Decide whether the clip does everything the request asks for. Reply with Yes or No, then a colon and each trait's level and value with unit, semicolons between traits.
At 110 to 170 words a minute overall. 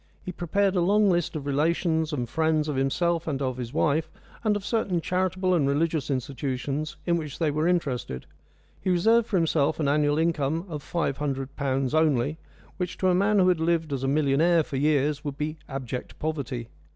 No: average, 195 wpm